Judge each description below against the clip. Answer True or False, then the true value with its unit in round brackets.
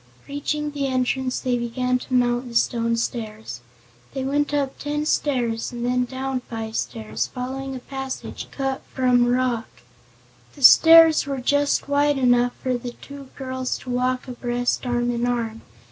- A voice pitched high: True (255 Hz)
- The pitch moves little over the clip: True (2.0 semitones)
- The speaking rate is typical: True (160 wpm)